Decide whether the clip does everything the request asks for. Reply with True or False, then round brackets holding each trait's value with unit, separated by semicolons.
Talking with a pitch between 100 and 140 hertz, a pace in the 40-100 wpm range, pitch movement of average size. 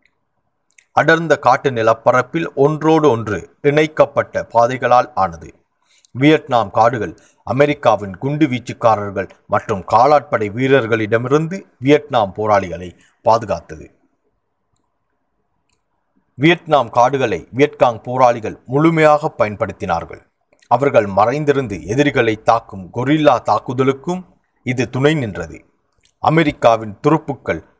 True (135 Hz; 75 wpm; 4.8 semitones)